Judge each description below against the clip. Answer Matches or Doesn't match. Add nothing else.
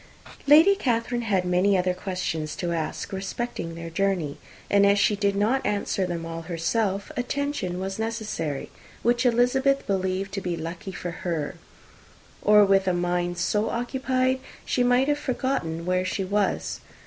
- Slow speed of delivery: Doesn't match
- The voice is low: Doesn't match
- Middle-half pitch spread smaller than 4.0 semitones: Doesn't match